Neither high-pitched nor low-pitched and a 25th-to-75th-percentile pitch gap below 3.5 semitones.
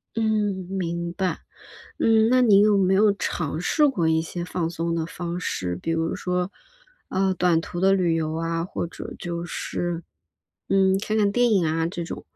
Yes: medium, 180 Hz; average, 2.8 semitones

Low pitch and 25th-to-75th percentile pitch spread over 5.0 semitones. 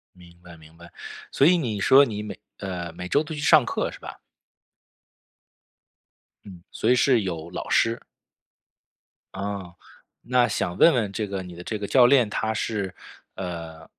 Yes: low, 100 Hz; wide, 5.6 semitones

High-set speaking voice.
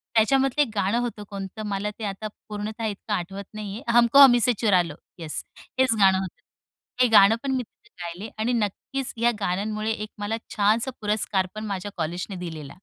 Yes: high, 210 Hz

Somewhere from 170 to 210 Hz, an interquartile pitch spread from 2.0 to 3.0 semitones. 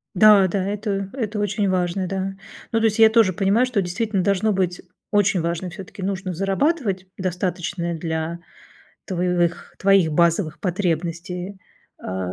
Yes: high, 190 Hz; narrow, 2.6 semitones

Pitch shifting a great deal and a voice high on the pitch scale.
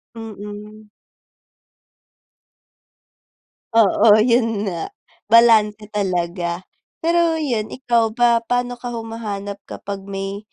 No: narrow, 2.6 semitones; high, 215 Hz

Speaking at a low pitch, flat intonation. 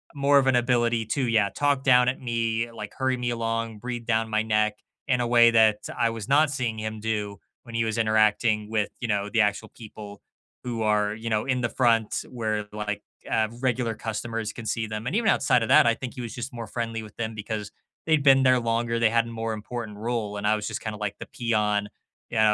Yes: low, 115 Hz; narrow, 2.0 semitones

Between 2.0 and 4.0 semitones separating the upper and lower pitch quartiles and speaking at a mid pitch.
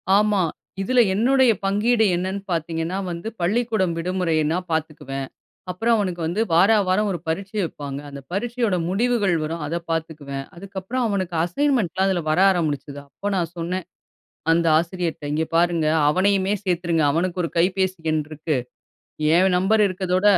Yes: average, 3.4 semitones; medium, 180 Hz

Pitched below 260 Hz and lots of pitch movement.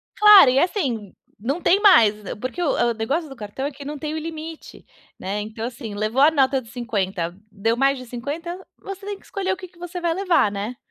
No: very high, 275 Hz; wide, 7.3 semitones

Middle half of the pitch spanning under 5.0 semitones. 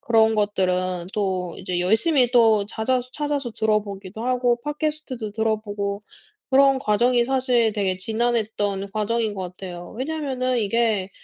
Yes: average, 3.8 semitones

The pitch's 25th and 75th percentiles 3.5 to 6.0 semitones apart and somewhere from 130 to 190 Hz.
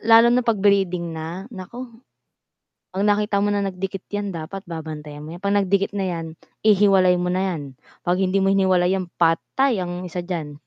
No: average, 2.7 semitones; medium, 185 Hz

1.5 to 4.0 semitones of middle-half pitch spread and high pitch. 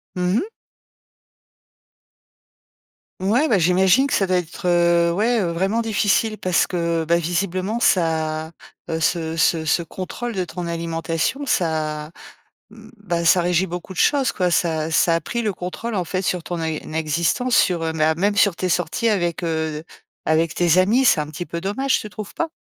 No: average, 3.7 semitones; medium, 175 Hz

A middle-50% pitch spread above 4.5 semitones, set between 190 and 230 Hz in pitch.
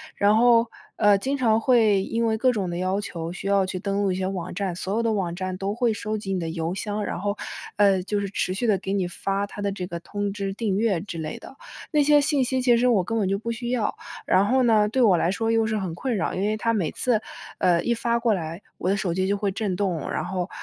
No: average, 3.3 semitones; high, 200 Hz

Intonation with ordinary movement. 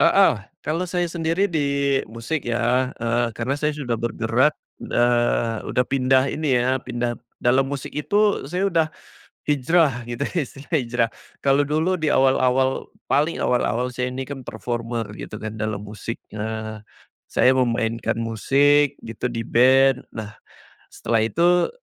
Yes: average, 3.7 semitones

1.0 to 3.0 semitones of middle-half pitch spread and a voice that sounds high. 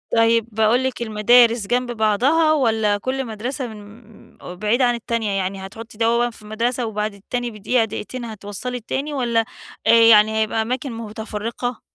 Yes: narrow, 2.4 semitones; high, 230 Hz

